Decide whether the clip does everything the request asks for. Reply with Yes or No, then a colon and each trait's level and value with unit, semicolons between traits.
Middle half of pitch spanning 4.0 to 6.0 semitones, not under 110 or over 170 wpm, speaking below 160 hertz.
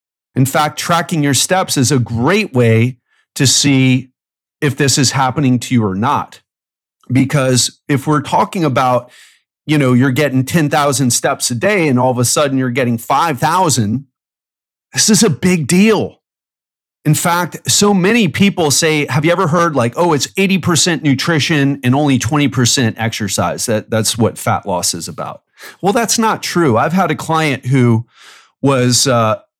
Yes: average, 5.0 semitones; average, 165 wpm; medium, 140 Hz